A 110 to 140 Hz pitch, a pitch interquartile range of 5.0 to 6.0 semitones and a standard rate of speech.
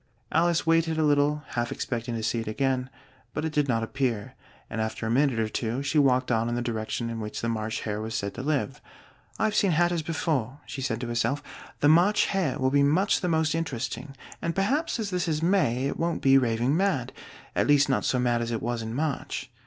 No: low, 135 Hz; average, 5.3 semitones; fast, 225 wpm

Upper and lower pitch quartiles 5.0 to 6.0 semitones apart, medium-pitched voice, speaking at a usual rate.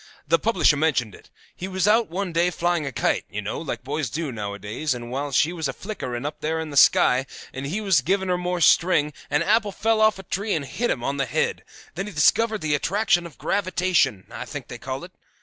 No: wide, 5.5 semitones; medium, 160 Hz; fast, 230 wpm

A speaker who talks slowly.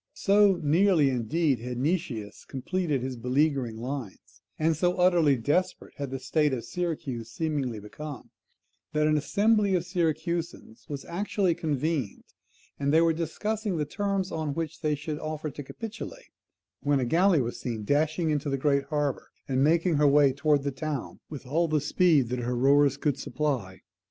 No: average, 170 wpm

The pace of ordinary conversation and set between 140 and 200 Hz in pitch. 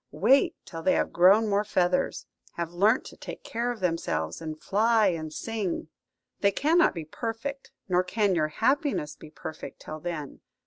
Yes: average, 170 wpm; medium, 185 Hz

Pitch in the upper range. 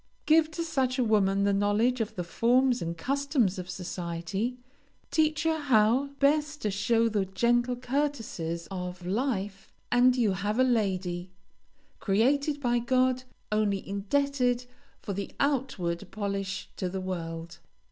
Yes: high, 220 Hz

